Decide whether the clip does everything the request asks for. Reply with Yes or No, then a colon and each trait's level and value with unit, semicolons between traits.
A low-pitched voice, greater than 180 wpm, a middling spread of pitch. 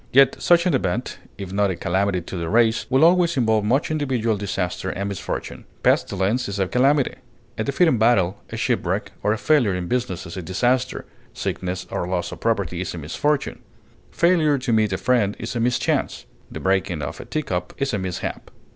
No: low, 110 Hz; average, 195 wpm; wide, 5.7 semitones